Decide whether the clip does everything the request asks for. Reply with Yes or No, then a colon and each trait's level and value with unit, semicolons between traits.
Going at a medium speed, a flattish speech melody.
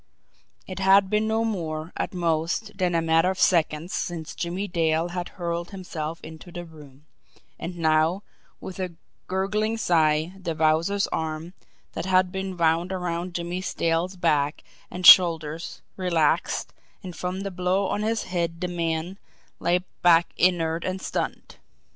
Yes: average, 150 wpm; narrow, 2.3 semitones